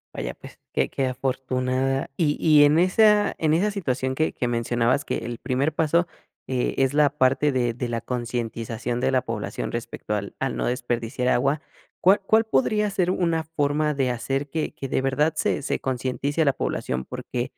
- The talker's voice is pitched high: No, low, 135 Hz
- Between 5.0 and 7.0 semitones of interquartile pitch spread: No, average, 4.1 semitones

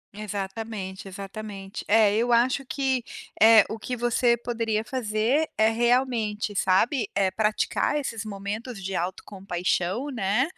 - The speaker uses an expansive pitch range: No, average, 3.3 semitones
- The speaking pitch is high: Yes, high, 220 Hz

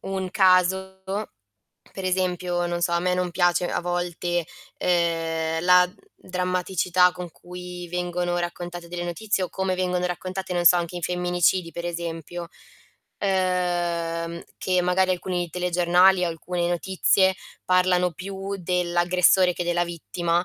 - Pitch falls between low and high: Yes, medium, 180 Hz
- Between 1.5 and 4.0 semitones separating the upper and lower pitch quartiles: No, narrow, 0.9 semitones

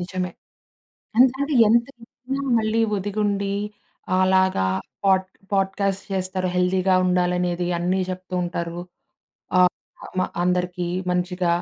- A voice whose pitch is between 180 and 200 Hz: Yes, medium, 185 Hz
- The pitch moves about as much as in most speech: No, narrow, 1.8 semitones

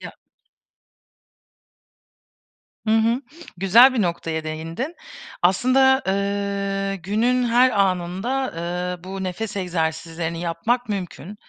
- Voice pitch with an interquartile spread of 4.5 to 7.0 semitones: Yes, average, 4.9 semitones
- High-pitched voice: Yes, high, 195 Hz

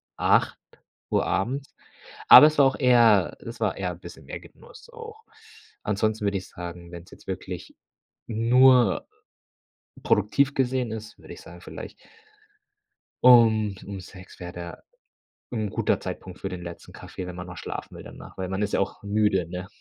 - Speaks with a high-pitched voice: No, low, 105 Hz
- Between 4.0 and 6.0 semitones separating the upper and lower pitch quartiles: Yes, average, 4.9 semitones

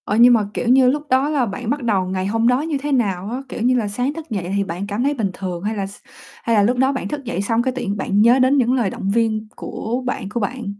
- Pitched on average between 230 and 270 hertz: Yes, high, 235 Hz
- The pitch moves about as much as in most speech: Yes, average, 4.3 semitones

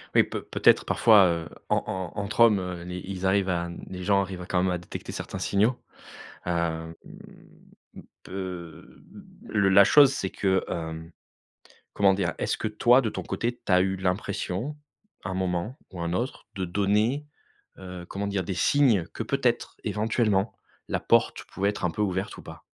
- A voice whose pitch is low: Yes, very low, 95 Hz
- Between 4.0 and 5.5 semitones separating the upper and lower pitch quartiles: No, average, 2.8 semitones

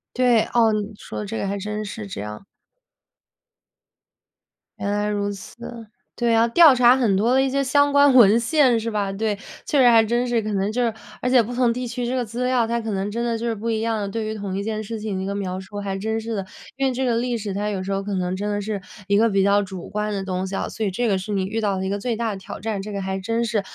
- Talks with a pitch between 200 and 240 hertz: Yes, high, 215 Hz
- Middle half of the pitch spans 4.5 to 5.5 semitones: No, average, 2.9 semitones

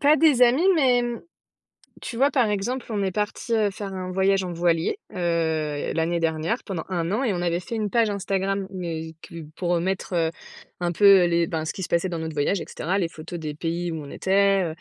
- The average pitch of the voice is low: No, medium, 185 Hz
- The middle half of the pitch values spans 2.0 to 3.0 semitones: No, average, 3.7 semitones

